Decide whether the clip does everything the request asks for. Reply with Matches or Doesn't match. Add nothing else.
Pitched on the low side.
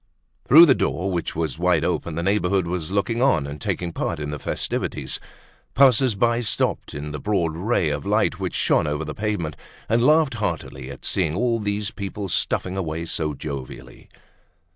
Matches